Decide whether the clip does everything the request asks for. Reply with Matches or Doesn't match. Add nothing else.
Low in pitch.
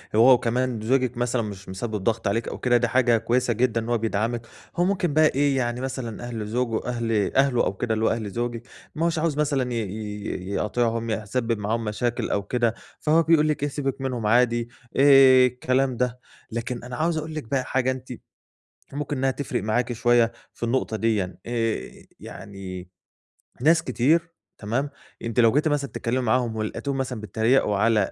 Matches